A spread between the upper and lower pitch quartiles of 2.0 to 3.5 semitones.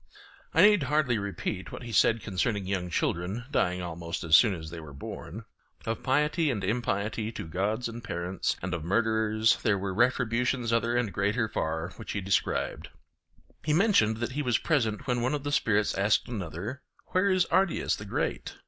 No: average, 4.7 semitones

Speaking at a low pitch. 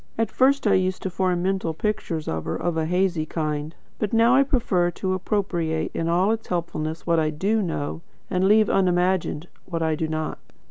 No: medium, 180 Hz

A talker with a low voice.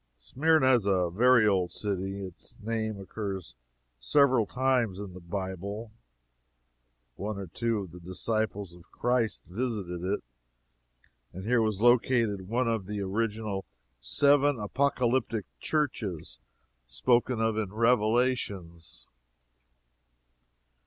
Yes: low, 105 Hz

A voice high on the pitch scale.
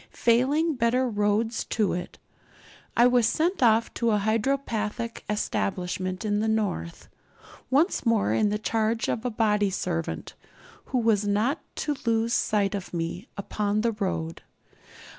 Yes: high, 220 Hz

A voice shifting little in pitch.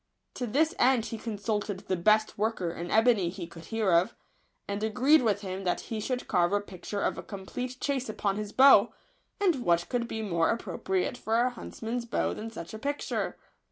No: average, 4.3 semitones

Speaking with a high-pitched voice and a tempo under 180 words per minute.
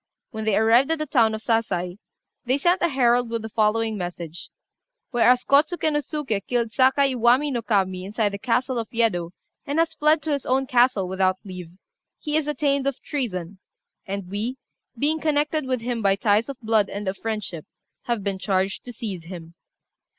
No: high, 230 Hz; average, 185 wpm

